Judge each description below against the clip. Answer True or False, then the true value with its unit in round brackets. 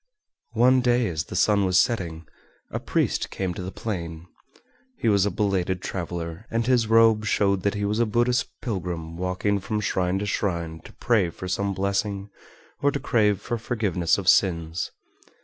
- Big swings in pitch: False (3.7 semitones)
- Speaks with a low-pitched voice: True (100 Hz)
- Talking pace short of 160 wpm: False (175 wpm)